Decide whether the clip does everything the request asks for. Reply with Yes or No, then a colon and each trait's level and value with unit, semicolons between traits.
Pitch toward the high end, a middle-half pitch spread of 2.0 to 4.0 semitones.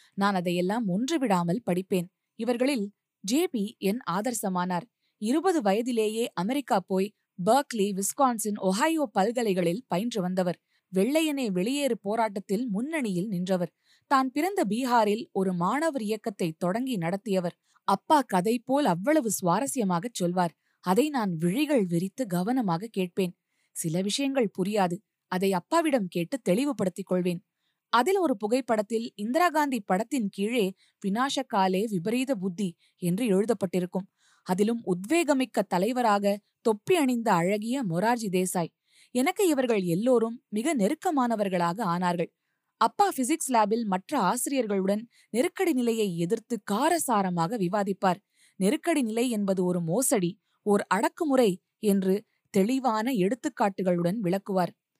No: high, 210 Hz; average, 5.3 semitones